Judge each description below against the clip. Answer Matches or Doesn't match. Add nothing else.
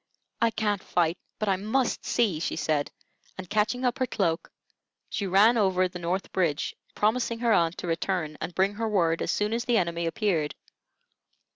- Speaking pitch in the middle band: Doesn't match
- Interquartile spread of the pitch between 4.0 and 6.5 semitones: Matches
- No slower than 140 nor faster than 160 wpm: Doesn't match